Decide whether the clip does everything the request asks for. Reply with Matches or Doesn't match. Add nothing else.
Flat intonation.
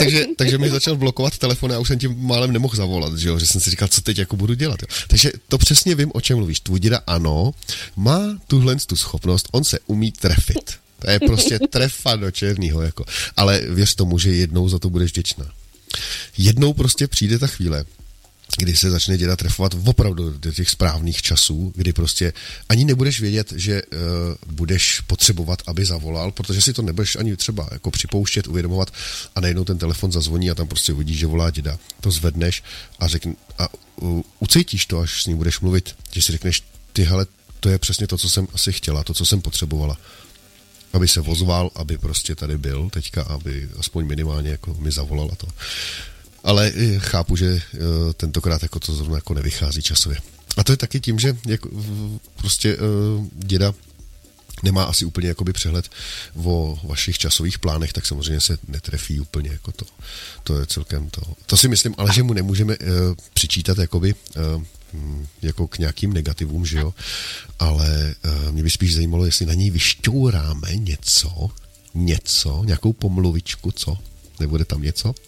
Doesn't match